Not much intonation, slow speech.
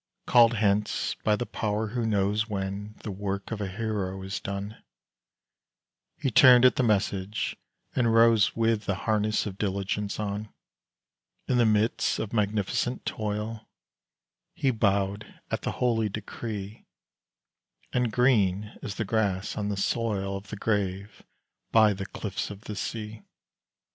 No: narrow, 2.2 semitones; average, 145 wpm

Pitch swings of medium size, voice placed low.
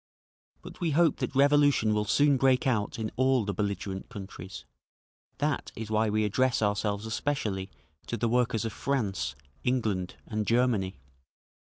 Yes: average, 4.2 semitones; low, 110 Hz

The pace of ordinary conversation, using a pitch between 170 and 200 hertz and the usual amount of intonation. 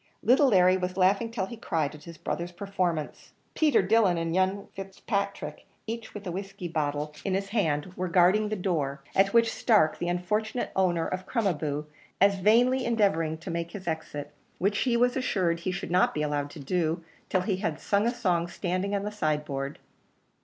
Yes: average, 195 wpm; medium, 185 Hz; average, 3.7 semitones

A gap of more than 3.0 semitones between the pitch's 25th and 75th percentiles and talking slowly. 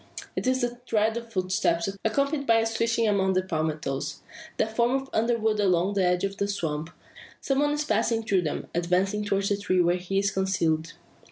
No: average, 4.2 semitones; average, 195 wpm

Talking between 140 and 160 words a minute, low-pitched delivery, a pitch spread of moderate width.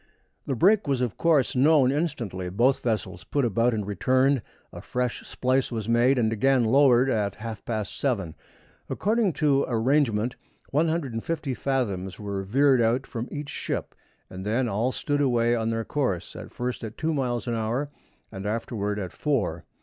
No: average, 170 wpm; low, 120 Hz; average, 4.0 semitones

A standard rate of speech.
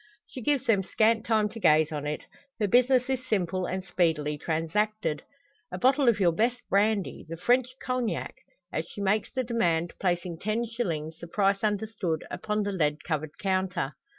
Yes: average, 175 wpm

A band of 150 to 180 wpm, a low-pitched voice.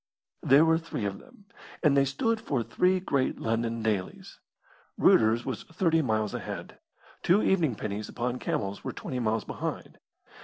Yes: average, 155 wpm; low, 125 Hz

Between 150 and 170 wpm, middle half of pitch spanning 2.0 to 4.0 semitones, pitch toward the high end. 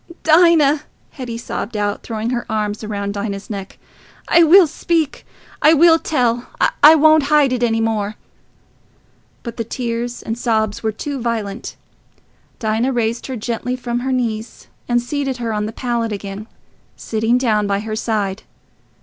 Yes: average, 160 wpm; average, 3.4 semitones; high, 235 Hz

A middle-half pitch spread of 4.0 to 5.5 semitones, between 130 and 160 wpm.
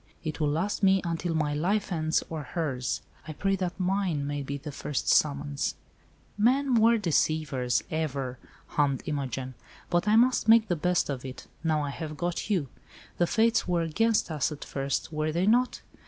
No: average, 5.1 semitones; average, 180 wpm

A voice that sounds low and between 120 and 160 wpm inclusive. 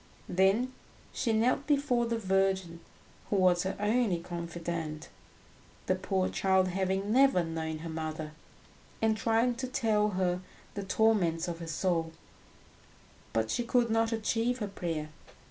No: high, 190 Hz; average, 140 wpm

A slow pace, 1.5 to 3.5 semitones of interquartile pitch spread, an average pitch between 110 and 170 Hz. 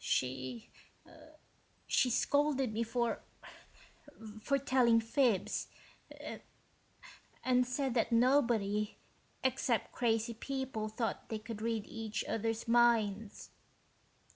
No: slow, 90 wpm; narrow, 2.6 semitones; high, 230 Hz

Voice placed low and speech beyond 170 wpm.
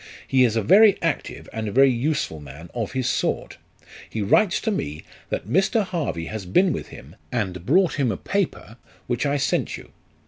Yes: low, 125 Hz; average, 185 wpm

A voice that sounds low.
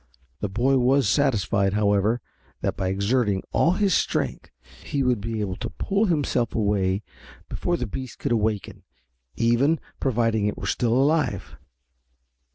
Yes: low, 115 Hz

